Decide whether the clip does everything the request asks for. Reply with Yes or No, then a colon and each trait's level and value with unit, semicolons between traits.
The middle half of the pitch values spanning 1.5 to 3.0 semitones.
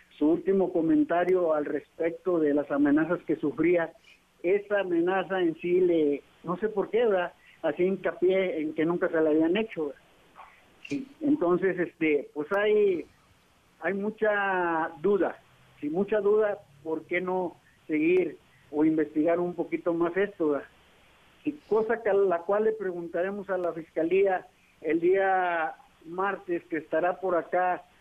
No: average, 3.4 semitones